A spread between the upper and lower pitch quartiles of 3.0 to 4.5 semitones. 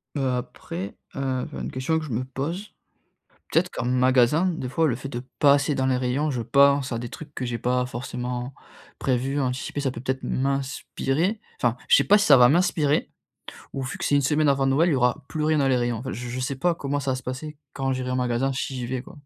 No: narrow, 2.4 semitones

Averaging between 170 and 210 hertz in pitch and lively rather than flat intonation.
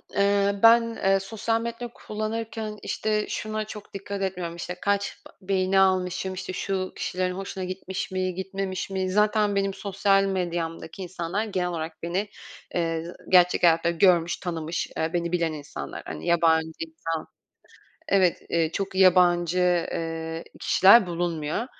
No: medium, 185 Hz; average, 2.7 semitones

